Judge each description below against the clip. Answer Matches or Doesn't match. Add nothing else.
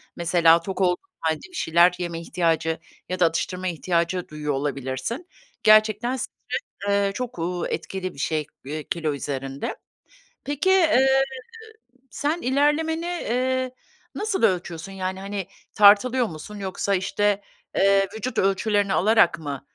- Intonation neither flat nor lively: Doesn't match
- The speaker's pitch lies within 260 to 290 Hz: Doesn't match